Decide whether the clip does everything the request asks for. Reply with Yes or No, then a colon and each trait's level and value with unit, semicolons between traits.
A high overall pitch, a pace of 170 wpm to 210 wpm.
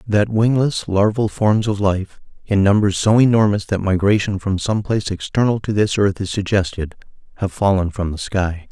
No: low, 100 Hz; average, 180 wpm